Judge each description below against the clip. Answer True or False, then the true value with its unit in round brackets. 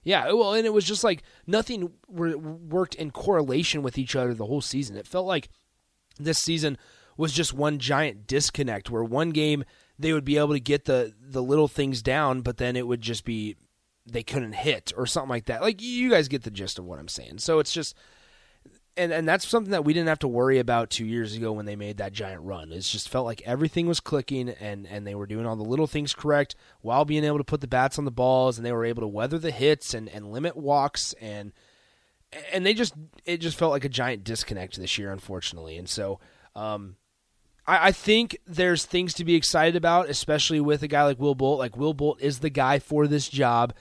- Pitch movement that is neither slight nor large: False (5.7 semitones)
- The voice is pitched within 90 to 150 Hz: True (140 Hz)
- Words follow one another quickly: True (230 wpm)